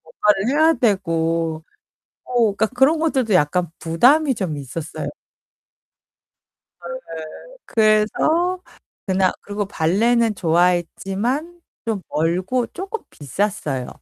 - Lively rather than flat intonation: Yes, wide, 7.2 semitones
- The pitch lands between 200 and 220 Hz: Yes, high, 205 Hz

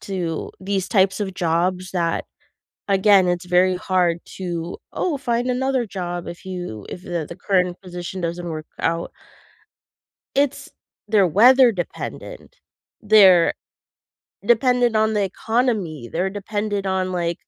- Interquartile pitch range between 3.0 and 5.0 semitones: Yes, average, 3.5 semitones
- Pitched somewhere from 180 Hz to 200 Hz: Yes, medium, 185 Hz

